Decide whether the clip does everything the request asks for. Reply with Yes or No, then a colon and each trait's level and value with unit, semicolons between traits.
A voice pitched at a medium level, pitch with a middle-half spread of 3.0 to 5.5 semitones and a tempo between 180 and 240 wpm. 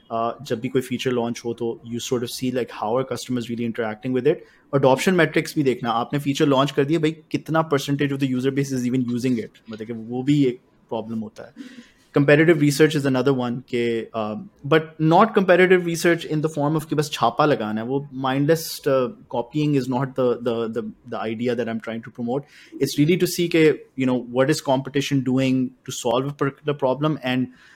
No: low, 130 Hz; average, 3.7 semitones; fast, 205 wpm